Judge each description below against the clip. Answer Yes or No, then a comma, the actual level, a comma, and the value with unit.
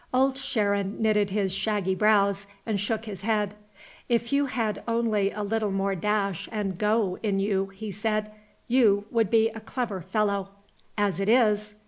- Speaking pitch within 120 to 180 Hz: No, high, 210 Hz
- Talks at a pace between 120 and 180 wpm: Yes, average, 165 wpm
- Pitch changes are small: Yes, narrow, 2.1 semitones